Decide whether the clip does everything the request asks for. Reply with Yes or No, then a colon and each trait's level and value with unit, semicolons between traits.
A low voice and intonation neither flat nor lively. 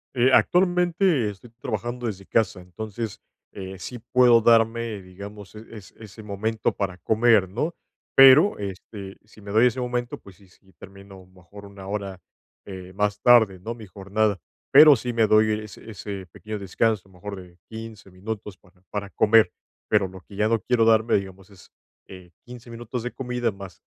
Yes: low, 105 Hz; average, 3.2 semitones